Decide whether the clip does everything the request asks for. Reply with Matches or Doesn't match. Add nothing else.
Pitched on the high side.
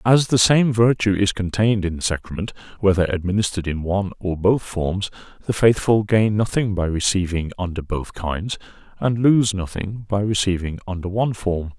Doesn't match